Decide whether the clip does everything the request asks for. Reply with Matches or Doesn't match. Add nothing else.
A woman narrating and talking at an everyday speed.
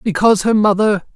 Matches